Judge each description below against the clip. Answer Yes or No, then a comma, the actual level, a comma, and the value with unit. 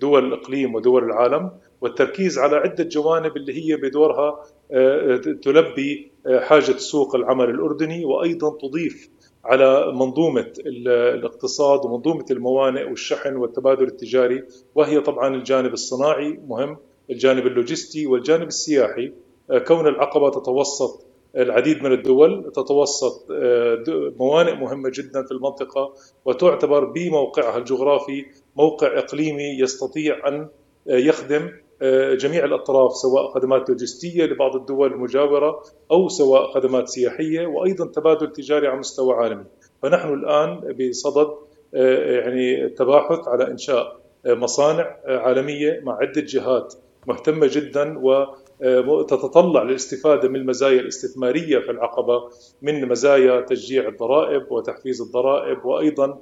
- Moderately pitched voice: Yes, medium, 145 Hz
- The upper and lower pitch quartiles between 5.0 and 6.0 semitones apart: No, average, 4.2 semitones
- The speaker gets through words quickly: No, average, 110 wpm